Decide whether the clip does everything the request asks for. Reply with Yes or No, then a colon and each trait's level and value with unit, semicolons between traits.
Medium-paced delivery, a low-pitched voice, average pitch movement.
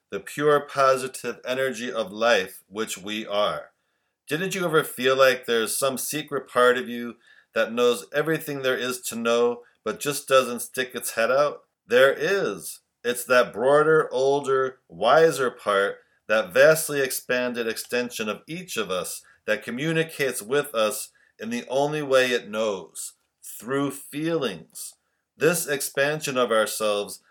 Yes: average, 145 wpm; low, 130 Hz; average, 3.4 semitones